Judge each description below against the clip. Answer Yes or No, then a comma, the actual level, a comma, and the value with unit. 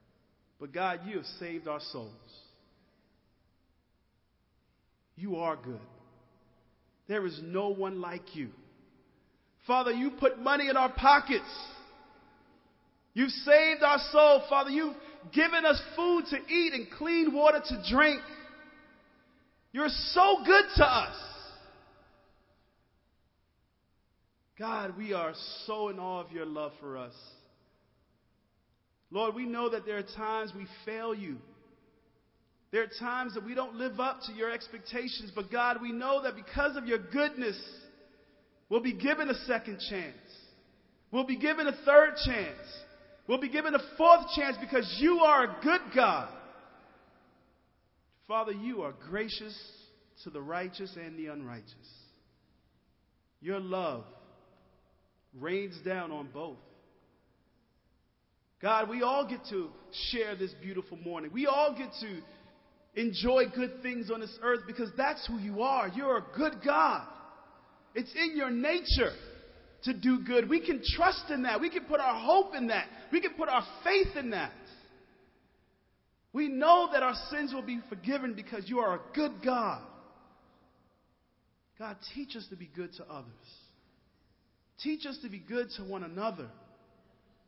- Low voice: No, high, 240 Hz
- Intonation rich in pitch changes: Yes, wide, 6.8 semitones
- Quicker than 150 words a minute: No, average, 145 wpm